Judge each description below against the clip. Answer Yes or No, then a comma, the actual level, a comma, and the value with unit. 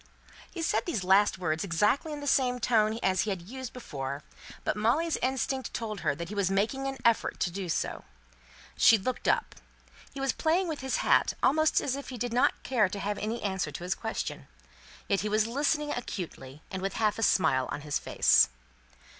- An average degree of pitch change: No, wide, 5.8 semitones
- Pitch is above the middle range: Yes, high, 215 Hz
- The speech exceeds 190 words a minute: Yes, fast, 205 wpm